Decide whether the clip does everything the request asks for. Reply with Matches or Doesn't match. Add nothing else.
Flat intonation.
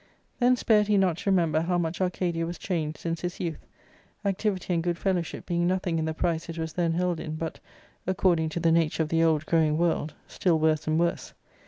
Matches